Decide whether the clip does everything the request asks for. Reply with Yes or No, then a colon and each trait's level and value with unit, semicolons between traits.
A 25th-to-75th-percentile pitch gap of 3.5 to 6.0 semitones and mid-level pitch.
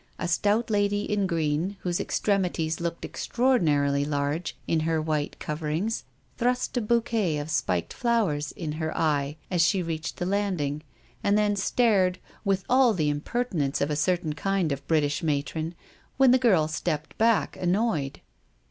Yes: average, 5.3 semitones; medium, 170 Hz